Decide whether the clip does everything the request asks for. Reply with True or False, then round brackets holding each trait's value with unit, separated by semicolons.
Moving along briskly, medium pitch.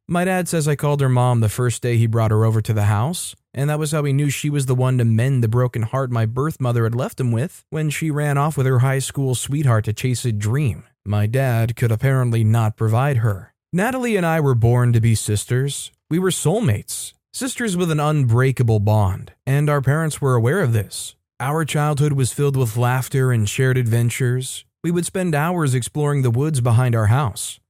False (220 wpm; 130 Hz)